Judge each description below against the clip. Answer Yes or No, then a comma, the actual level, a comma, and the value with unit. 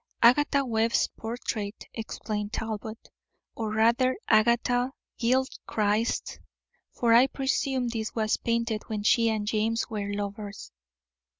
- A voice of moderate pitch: No, high, 225 Hz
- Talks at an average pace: No, slow, 110 wpm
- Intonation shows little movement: Yes, narrow, 2.0 semitones